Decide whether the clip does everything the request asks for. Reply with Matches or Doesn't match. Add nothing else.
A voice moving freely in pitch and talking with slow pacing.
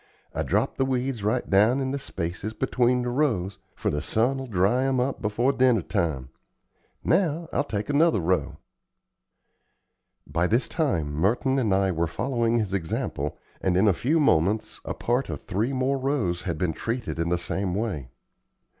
Doesn't match